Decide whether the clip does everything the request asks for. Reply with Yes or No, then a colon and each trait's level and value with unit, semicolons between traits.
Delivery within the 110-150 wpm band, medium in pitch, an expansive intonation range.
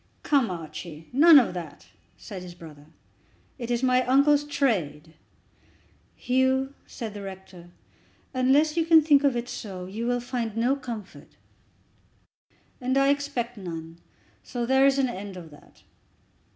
No: average, 145 wpm; high, 240 Hz; wide, 6.8 semitones